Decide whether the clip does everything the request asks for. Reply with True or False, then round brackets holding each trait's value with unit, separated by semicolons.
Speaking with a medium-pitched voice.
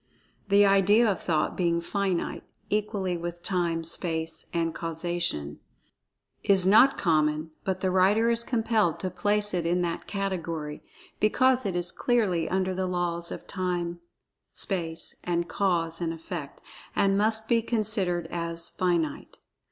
True (180 Hz)